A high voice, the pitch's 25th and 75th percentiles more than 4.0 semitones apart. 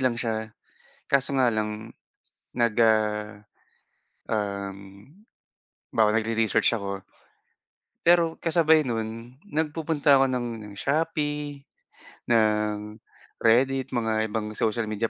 No: low, 115 Hz; average, 4.4 semitones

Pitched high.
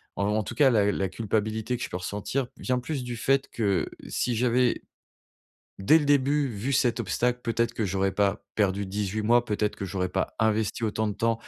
No: low, 110 Hz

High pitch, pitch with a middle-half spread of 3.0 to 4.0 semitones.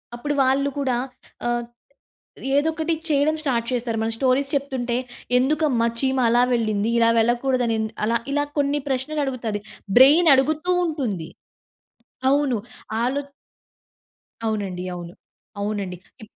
Yes: very high, 255 Hz; average, 3.7 semitones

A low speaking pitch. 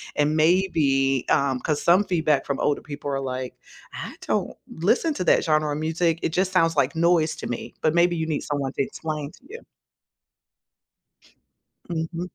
No: medium, 155 Hz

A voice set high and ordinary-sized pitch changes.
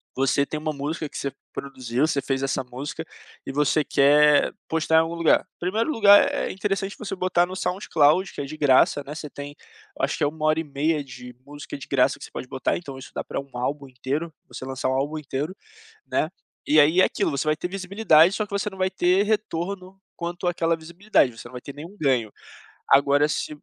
No: medium, 155 Hz; average, 4.3 semitones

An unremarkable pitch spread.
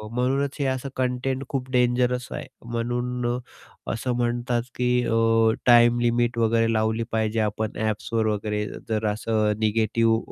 No: narrow, 1.9 semitones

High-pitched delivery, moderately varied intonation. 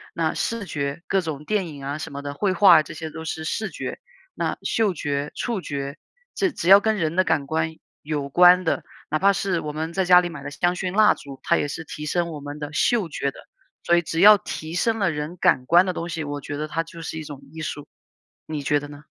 No: medium, 160 Hz; average, 3.6 semitones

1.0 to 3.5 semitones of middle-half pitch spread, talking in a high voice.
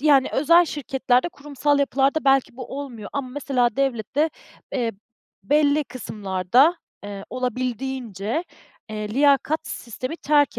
Yes: average, 3.2 semitones; very high, 270 Hz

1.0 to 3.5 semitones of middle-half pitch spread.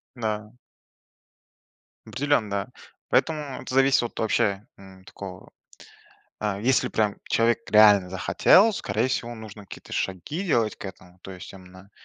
No: average, 4.1 semitones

